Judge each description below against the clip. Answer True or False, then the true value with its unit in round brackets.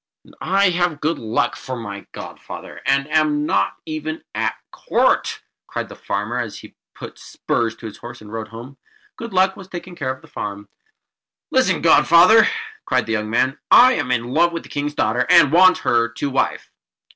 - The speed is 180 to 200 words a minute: True (190 wpm)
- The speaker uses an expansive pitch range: True (6.8 semitones)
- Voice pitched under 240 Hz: True (135 Hz)